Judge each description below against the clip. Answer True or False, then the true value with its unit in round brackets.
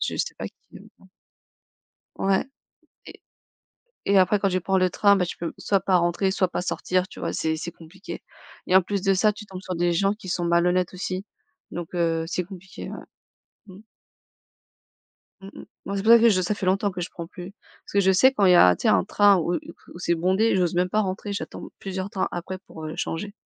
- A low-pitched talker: False (185 Hz)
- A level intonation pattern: True (2.1 semitones)